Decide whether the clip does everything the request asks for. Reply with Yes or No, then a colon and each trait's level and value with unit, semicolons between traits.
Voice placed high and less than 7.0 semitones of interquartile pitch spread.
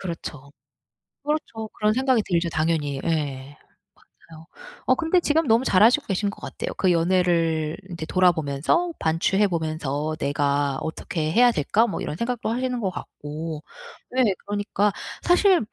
No: medium, 175 Hz; wide, 6.5 semitones